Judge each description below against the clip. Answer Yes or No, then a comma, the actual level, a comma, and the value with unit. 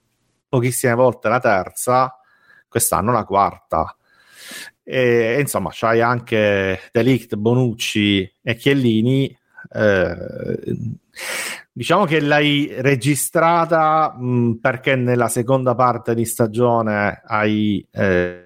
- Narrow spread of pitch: No, average, 3.0 semitones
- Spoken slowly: Yes, slow, 100 wpm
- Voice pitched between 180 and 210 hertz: No, low, 120 Hz